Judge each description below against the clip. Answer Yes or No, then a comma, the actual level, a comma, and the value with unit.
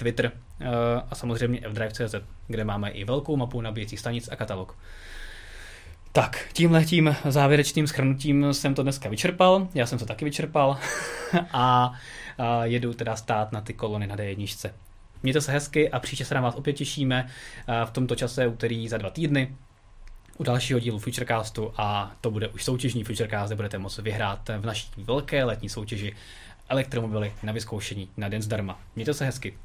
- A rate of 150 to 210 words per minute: Yes, fast, 170 wpm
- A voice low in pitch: Yes, low, 115 Hz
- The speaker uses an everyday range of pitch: Yes, average, 4.1 semitones